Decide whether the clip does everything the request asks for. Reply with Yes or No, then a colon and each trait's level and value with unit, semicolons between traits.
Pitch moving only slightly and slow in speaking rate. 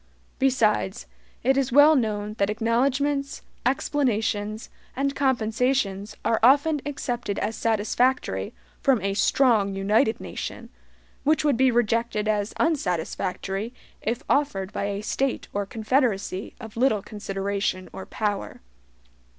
No: average, 4.7 semitones; slow, 120 wpm